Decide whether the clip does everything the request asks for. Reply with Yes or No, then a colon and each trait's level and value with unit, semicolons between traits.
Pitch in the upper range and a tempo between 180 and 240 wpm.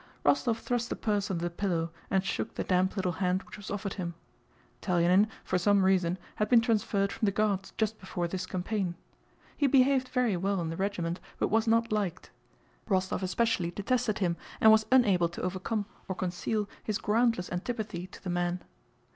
Yes: high, 195 Hz; average, 185 wpm